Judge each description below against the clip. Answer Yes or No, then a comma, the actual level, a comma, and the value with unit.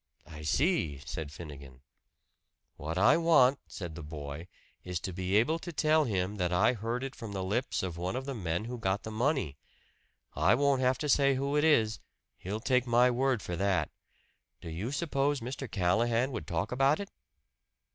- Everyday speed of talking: Yes, average, 185 wpm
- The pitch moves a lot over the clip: Yes, wide, 7.2 semitones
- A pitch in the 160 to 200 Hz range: No, low, 115 Hz